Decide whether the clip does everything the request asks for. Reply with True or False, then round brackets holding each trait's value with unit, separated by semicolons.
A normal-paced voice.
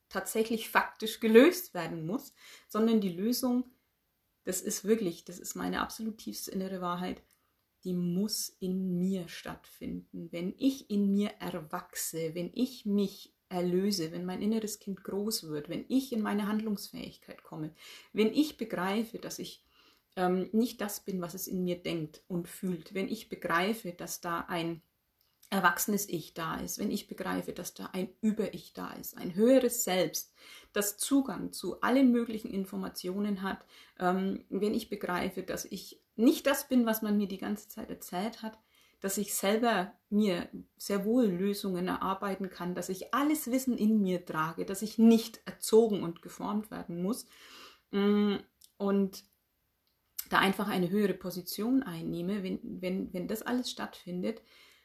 True (155 wpm)